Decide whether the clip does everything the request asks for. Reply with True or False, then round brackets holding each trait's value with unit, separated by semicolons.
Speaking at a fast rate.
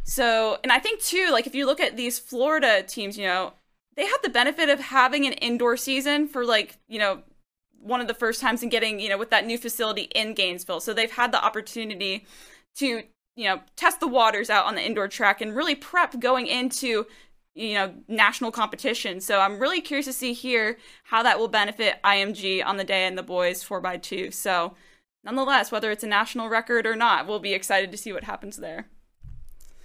True (215 wpm)